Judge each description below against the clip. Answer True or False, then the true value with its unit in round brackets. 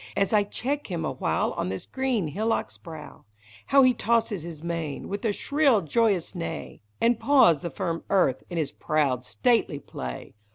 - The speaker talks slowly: False (175 wpm)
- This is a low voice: False (185 Hz)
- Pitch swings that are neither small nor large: False (6.8 semitones)